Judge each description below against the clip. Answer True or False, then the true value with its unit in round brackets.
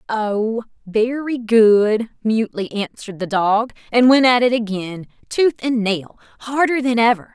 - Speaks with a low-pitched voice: False (225 Hz)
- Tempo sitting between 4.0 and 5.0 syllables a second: True (4.2 syllables/s)